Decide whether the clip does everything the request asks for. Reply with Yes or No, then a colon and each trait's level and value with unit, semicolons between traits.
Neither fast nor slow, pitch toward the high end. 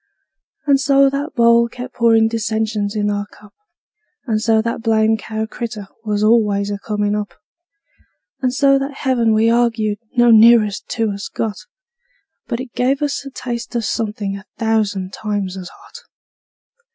Yes: average, 160 wpm; high, 225 Hz